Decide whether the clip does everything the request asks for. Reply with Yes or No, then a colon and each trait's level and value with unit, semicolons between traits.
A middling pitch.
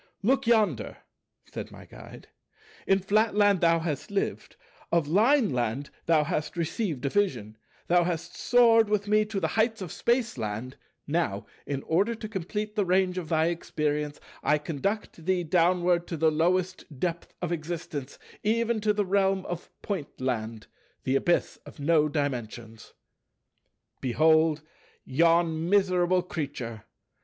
Yes: medium, 170 Hz